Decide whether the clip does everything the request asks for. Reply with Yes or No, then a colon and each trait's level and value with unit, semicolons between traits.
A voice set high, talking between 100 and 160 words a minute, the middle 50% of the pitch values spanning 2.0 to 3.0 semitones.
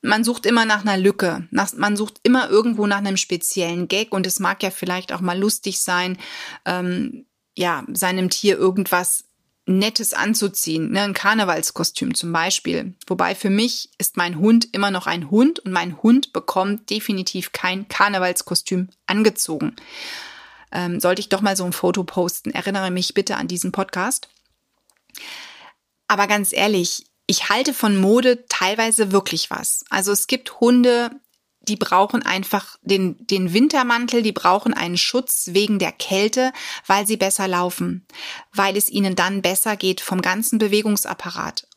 No: high, 200 Hz; average, 155 wpm; average, 3.5 semitones